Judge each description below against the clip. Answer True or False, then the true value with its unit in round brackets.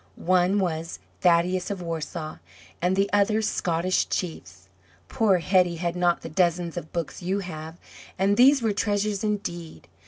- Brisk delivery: False (150 wpm)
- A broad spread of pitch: False (3.0 semitones)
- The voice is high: False (180 Hz)